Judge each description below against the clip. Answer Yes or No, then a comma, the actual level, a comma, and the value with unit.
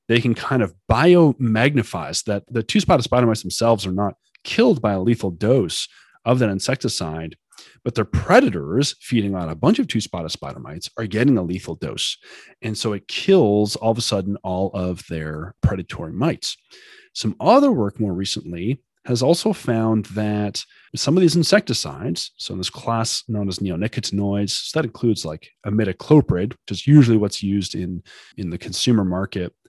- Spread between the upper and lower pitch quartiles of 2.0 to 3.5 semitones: No, average, 4.6 semitones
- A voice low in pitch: Yes, low, 110 Hz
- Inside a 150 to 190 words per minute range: Yes, average, 175 wpm